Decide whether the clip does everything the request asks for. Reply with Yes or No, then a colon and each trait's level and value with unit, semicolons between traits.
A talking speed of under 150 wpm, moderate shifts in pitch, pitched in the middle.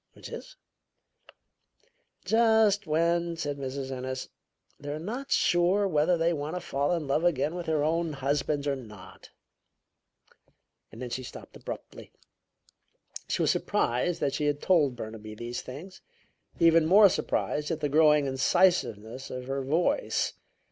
Yes: average, 140 wpm; average, 4.5 semitones; medium, 150 Hz